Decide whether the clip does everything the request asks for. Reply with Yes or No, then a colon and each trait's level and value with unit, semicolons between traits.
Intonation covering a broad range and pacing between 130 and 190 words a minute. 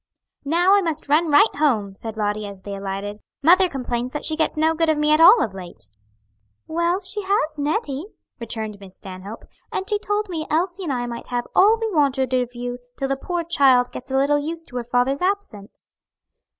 No: wide, 6.2 semitones; fast, 205 wpm